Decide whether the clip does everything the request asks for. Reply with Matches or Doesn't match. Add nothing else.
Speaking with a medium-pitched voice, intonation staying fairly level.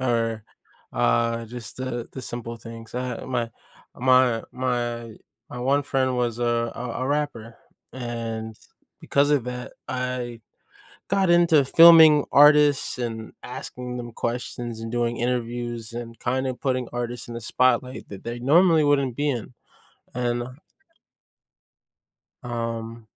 Doesn't match